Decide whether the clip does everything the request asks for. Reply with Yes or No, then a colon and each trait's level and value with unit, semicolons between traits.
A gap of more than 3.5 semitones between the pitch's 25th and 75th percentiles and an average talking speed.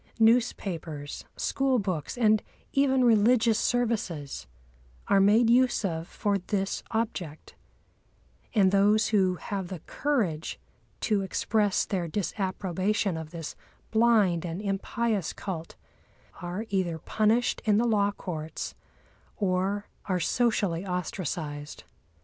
No: average, 4.0 semitones; slow, 110 wpm